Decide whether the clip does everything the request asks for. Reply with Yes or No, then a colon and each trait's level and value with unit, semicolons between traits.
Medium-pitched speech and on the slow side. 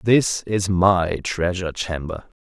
No: very low, 90 Hz; slow, 125 wpm